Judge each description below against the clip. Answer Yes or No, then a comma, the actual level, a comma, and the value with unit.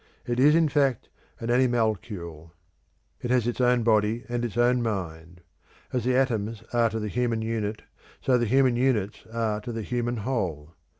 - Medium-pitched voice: No, low, 115 Hz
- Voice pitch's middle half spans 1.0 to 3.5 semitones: Yes, average, 2.7 semitones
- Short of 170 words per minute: No, average, 175 wpm